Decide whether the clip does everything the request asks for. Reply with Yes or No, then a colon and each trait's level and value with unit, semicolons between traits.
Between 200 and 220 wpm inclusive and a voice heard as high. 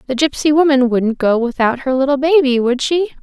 Yes: fast, 205 wpm; very high, 270 Hz